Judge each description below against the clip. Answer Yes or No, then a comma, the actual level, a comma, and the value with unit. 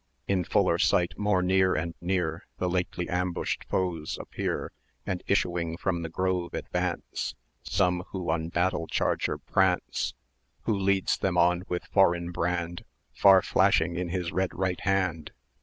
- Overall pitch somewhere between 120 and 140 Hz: No, very low, 90 Hz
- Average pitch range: No, narrow, 1.5 semitones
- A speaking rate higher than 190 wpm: No, average, 145 wpm